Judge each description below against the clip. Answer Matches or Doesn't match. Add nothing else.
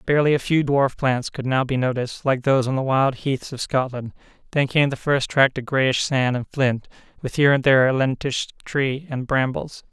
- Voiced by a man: Matches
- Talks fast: Matches